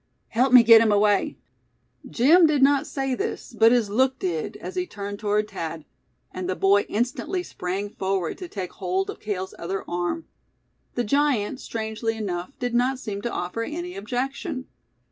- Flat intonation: No, average, 5.0 semitones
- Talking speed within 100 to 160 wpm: No, average, 170 wpm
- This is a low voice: No, high, 220 Hz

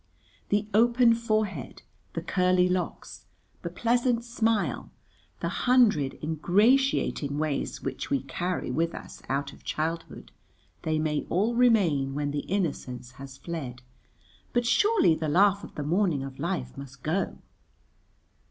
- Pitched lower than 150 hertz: No, medium, 170 Hz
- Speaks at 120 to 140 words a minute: Yes, slow, 135 wpm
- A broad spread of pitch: Yes, wide, 7.4 semitones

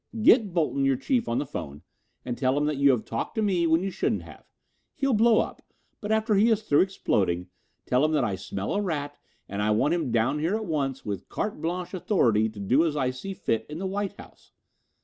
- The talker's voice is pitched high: No, medium, 150 Hz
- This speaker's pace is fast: Yes, fast, 235 wpm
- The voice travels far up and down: Yes, wide, 7.9 semitones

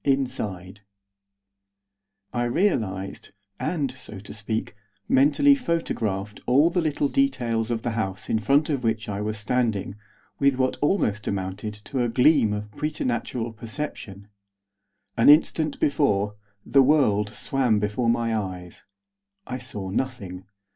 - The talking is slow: Yes, slow, 130 wpm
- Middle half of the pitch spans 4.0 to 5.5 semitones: Yes, average, 5.0 semitones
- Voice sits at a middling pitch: No, low, 115 Hz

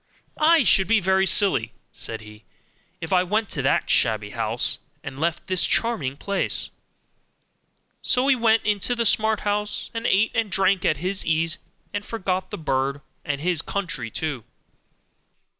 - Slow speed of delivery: No, average, 160 wpm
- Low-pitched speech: No, medium, 185 Hz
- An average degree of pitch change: No, wide, 6.8 semitones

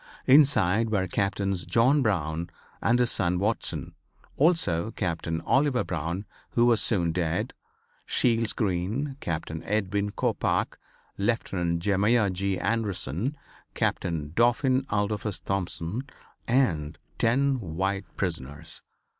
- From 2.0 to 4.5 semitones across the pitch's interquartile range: No, average, 5.2 semitones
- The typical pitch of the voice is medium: No, low, 100 Hz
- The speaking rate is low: Yes, slow, 105 wpm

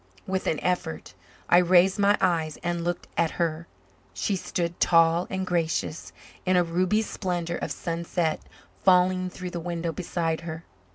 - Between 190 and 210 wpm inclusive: No, average, 155 wpm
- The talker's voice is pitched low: No, medium, 175 Hz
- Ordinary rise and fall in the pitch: No, narrow, 1.6 semitones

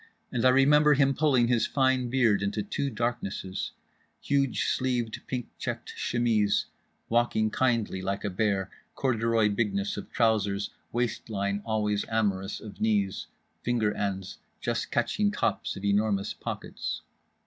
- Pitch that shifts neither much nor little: Yes, average, 3.4 semitones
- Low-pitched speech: Yes, low, 110 Hz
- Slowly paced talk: Yes, slow, 115 wpm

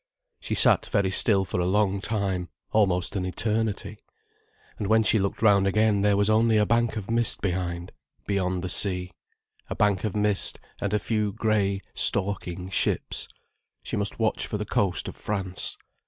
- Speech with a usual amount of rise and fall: No, narrow, 2.3 semitones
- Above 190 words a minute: No, average, 170 wpm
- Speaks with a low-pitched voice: Yes, low, 100 Hz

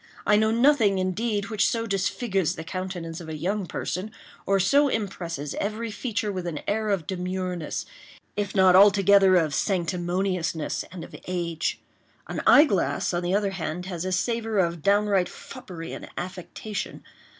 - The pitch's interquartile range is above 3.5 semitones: No, average, 2.9 semitones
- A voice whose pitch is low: No, high, 190 Hz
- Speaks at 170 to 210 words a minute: No, average, 155 wpm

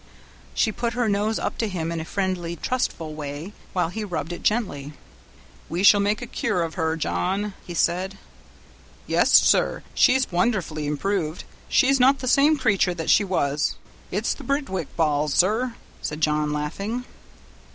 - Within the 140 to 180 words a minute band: Yes, average, 160 wpm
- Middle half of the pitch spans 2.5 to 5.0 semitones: No, wide, 5.6 semitones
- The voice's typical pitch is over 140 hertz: Yes, medium, 185 Hz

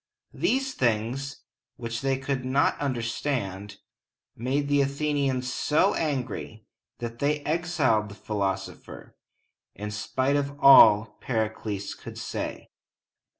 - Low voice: Yes, low, 130 Hz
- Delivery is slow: Yes, slow, 110 wpm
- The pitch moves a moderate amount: Yes, average, 4.5 semitones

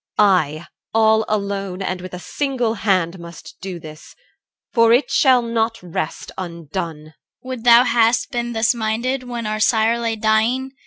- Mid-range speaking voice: No, high, 220 Hz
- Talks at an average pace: Yes, average, 160 wpm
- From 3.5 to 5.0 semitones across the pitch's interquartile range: Yes, average, 4.4 semitones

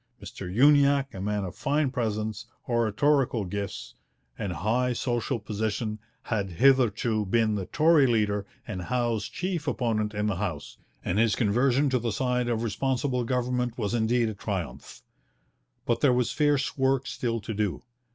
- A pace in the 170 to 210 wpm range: No, average, 155 wpm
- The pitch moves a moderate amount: Yes, average, 3.4 semitones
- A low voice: Yes, low, 115 Hz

